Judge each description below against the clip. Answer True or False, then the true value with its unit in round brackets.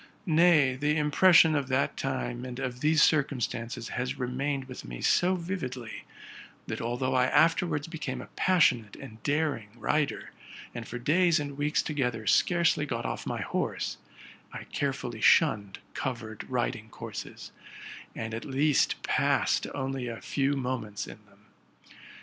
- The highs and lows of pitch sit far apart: False (3.8 semitones)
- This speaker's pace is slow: False (145 wpm)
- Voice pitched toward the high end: False (135 Hz)